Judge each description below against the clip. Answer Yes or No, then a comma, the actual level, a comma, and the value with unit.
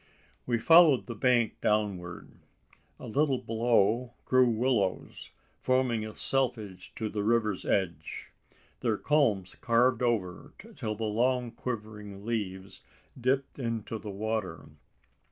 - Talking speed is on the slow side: Yes, slow, 120 wpm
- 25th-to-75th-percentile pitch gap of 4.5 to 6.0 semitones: No, average, 3.3 semitones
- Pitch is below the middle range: Yes, low, 115 Hz